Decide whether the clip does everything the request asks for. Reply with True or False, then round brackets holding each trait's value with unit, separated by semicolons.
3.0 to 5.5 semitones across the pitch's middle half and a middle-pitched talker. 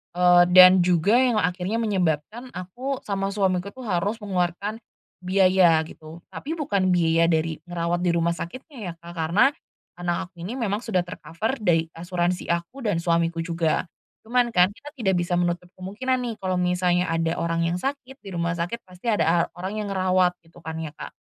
True (3.4 semitones; 180 Hz)